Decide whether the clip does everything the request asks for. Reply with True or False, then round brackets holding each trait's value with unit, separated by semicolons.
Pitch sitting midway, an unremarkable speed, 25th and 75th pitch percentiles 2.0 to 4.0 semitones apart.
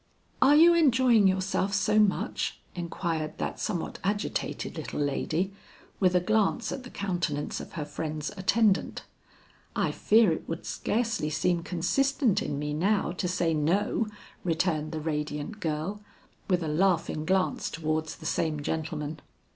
False (180 Hz; 145 wpm; 4.9 semitones)